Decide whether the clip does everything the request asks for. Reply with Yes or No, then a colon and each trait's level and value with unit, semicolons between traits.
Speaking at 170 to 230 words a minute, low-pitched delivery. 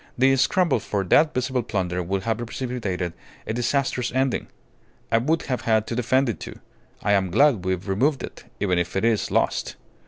Yes: average, 185 wpm; low, 115 Hz